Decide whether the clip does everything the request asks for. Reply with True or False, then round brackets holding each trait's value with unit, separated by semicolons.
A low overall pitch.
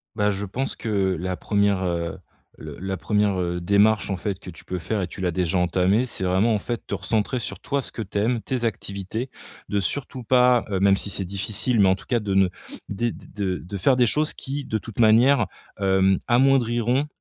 True (100 Hz)